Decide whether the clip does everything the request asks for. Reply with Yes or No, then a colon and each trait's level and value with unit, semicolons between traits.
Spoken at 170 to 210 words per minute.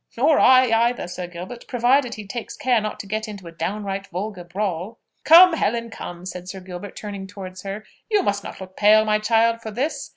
Yes: fast, 205 wpm